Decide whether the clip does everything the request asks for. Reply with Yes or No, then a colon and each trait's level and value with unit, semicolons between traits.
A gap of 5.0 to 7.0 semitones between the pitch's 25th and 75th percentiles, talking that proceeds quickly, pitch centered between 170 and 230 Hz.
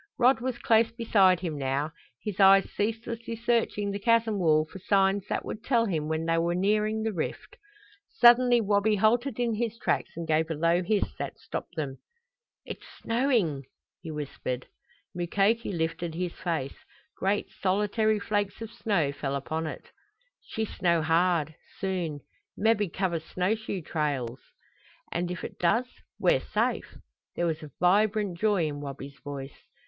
No: average, 5.3 semitones; average, 155 wpm; high, 190 Hz